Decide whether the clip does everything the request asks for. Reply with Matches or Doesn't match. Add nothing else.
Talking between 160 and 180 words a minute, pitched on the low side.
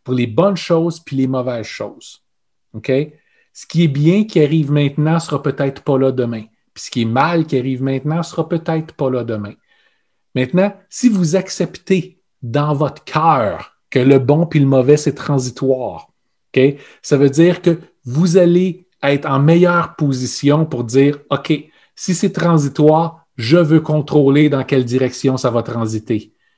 Doesn't match